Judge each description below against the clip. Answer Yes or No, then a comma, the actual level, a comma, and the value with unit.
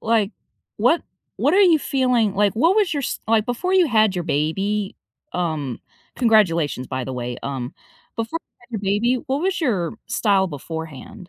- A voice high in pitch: Yes, high, 210 Hz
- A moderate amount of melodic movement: No, wide, 7.3 semitones